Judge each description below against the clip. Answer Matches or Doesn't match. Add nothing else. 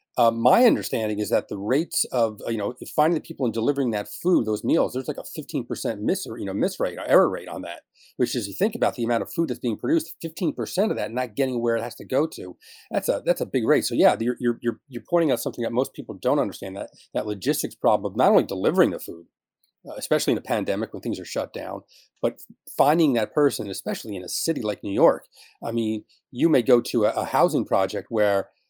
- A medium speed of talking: Doesn't match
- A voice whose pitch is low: Matches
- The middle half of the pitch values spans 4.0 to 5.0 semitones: Matches